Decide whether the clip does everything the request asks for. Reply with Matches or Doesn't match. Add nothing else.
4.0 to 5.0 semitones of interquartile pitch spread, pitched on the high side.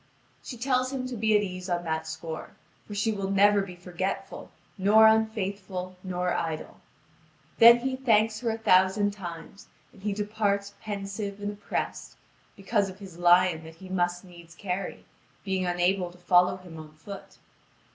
Doesn't match